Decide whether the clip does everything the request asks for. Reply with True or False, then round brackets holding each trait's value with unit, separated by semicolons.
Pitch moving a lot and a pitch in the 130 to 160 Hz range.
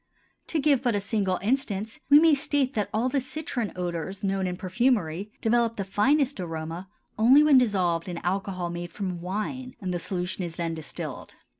False (6.0 semitones; 200 Hz)